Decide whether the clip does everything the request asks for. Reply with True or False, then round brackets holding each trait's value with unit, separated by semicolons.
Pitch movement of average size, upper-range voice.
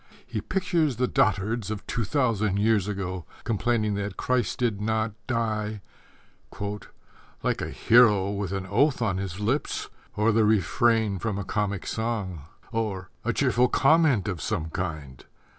False (3.1 semitones; 105 Hz)